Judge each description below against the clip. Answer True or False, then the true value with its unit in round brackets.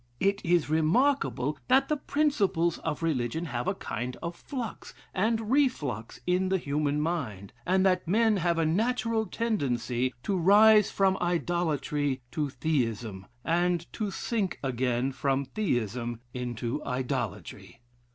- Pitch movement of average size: False (7.5 semitones)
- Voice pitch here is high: False (165 Hz)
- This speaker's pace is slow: True (130 wpm)